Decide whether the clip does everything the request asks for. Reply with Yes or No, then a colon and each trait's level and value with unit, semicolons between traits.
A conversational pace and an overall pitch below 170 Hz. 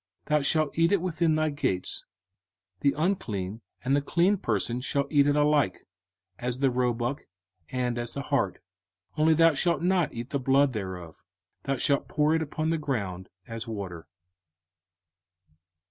Yes: average, 160 wpm; medium, 140 Hz